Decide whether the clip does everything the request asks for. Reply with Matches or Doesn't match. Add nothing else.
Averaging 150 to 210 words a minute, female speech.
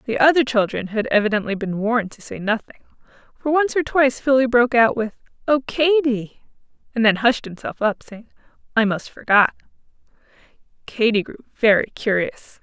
Matches